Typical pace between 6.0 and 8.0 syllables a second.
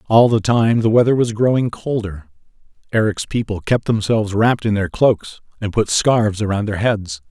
No: 5.0 syllables/s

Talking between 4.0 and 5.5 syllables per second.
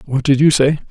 No: 6.0 syllables/s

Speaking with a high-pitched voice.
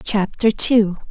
Yes: high, 210 Hz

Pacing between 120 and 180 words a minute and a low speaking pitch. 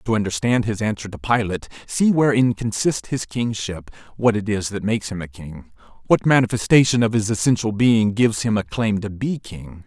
No: average, 195 wpm; low, 110 Hz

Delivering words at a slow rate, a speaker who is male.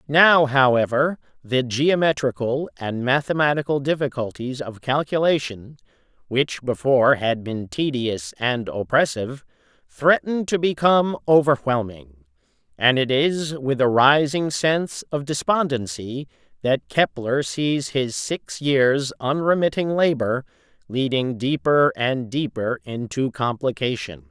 Yes: slow, 105 wpm; male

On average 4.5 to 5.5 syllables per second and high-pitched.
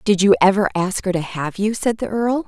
Yes: 5.3 syllables/s; high, 200 Hz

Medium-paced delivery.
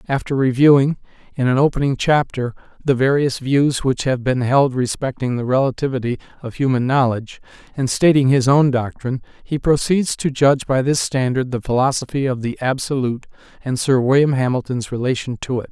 Yes: average, 165 wpm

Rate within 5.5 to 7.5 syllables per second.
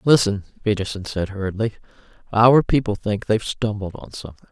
Yes: 5.9 syllables/s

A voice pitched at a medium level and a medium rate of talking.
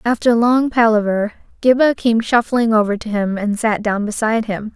No: high, 225 Hz; average, 175 wpm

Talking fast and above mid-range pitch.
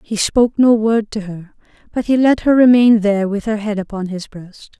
Yes: fast, 225 wpm; high, 215 Hz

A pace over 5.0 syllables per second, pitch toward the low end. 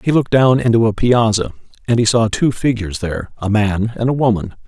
Yes: 6.0 syllables/s; low, 115 Hz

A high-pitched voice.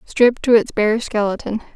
Yes: high, 220 Hz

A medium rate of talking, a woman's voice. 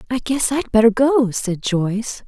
Yes: average, 185 wpm; female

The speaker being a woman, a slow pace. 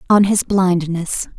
Yes: female; slow, 130 wpm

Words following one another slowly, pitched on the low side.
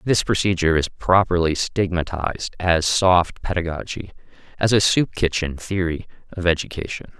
Yes: slow, 125 wpm; very low, 90 Hz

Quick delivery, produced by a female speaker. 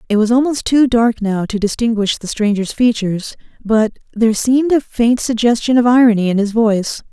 No: average, 185 wpm; female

